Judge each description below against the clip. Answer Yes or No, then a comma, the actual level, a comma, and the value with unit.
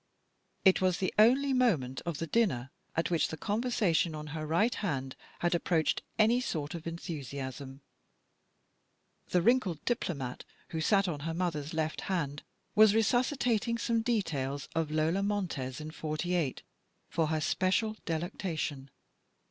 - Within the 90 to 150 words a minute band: Yes, average, 140 wpm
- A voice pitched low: No, medium, 170 Hz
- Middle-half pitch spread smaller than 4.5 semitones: No, wide, 5.5 semitones